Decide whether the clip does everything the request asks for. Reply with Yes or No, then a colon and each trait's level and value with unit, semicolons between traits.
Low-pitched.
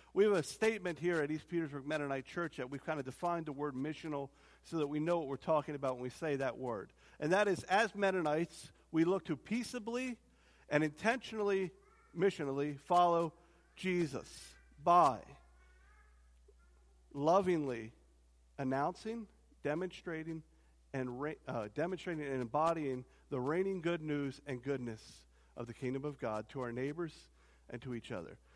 No: medium, 150 Hz